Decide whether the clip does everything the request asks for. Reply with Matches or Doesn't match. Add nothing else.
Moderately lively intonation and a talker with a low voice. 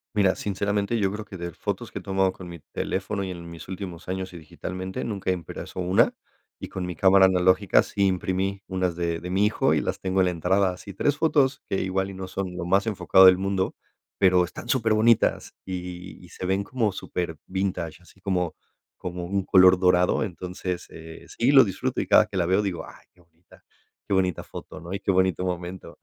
Doesn't match